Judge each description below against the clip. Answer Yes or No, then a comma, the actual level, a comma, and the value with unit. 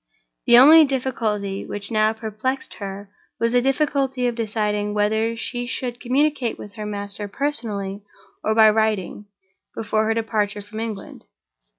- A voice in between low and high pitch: No, high, 220 Hz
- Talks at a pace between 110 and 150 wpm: Yes, average, 145 wpm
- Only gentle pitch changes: No, average, 3.0 semitones